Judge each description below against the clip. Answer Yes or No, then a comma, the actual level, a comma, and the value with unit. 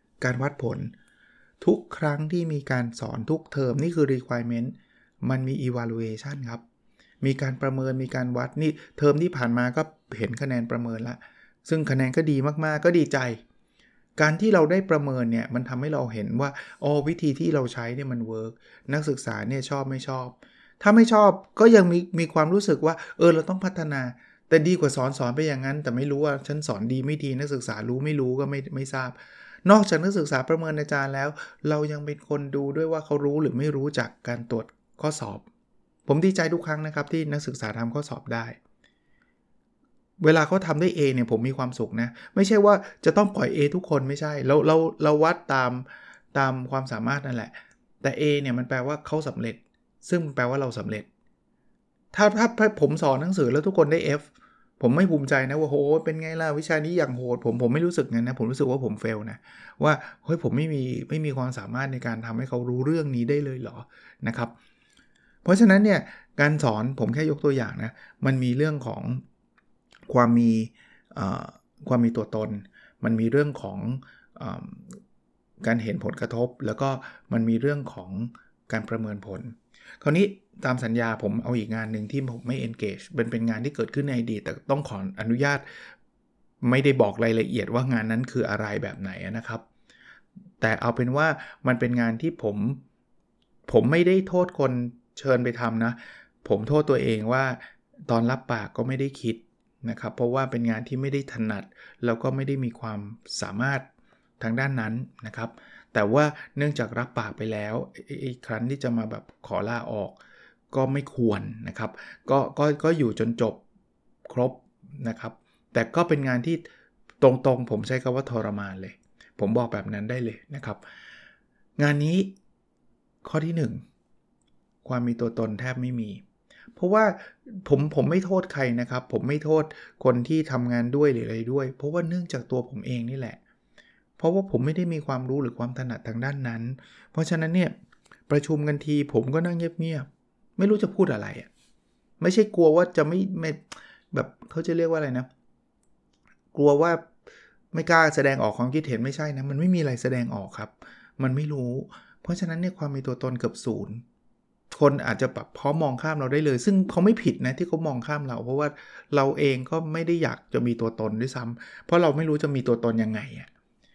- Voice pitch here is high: No, low, 135 Hz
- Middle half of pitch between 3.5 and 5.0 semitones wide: Yes, average, 4.5 semitones